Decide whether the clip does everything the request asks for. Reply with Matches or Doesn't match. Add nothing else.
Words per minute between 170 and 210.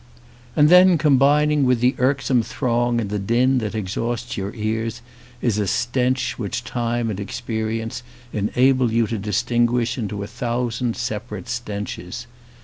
Doesn't match